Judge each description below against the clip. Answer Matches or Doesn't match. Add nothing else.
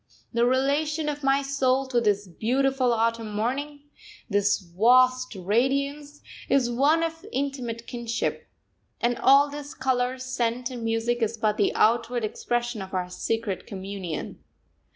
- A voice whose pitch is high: Matches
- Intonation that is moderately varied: Matches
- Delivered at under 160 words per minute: Matches